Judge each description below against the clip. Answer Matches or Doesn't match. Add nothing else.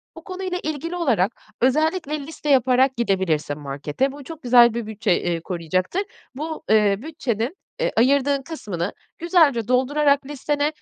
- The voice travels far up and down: Matches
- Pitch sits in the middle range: Doesn't match